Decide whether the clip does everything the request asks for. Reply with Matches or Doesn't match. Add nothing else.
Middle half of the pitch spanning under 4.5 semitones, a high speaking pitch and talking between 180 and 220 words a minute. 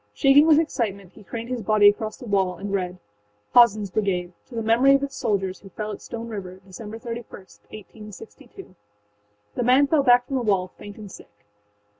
Matches